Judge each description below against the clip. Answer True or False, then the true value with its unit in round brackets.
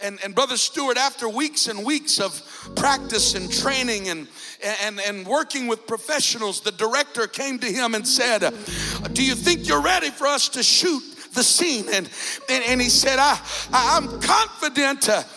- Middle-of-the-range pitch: False (255 Hz)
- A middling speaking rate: True (175 wpm)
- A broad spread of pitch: False (4.7 semitones)